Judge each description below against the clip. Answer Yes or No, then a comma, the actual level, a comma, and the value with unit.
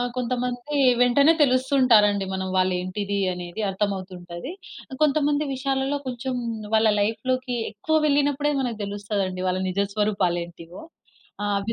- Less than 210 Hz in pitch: No, high, 220 Hz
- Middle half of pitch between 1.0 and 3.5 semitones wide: No, average, 5.1 semitones